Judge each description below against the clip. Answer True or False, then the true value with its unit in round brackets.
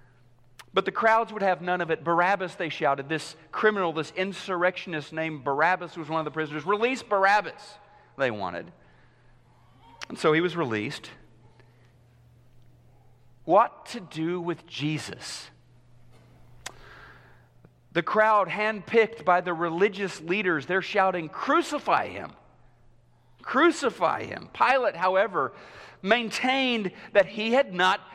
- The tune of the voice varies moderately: False (8.3 semitones)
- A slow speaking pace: True (120 wpm)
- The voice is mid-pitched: True (175 Hz)